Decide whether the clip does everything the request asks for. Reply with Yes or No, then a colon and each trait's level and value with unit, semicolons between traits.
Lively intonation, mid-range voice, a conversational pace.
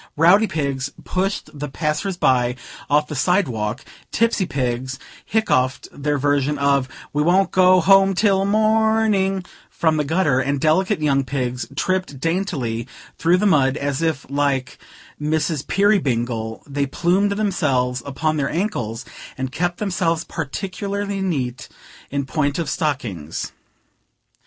No: wide, 5.9 semitones; medium, 150 Hz; slow, 130 wpm